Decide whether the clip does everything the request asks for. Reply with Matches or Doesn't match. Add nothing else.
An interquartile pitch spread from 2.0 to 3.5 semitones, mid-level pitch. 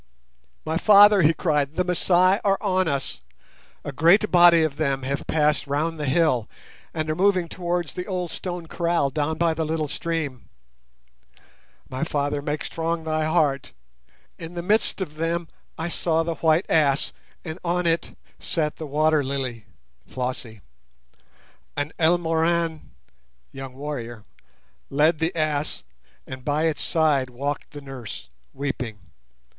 Matches